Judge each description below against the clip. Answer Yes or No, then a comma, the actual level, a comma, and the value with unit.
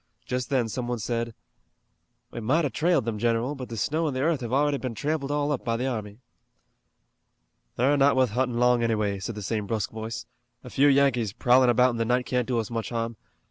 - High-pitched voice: No, low, 125 Hz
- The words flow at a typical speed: No, fast, 220 wpm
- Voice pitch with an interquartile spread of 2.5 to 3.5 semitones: Yes, average, 2.9 semitones